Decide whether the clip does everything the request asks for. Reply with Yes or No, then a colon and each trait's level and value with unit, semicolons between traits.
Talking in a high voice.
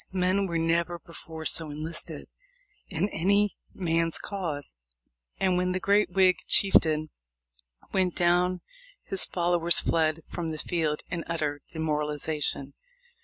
No: medium, 170 Hz